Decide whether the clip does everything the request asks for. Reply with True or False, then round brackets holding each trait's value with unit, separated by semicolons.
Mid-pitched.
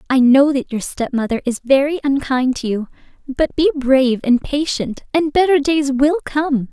False (275 Hz)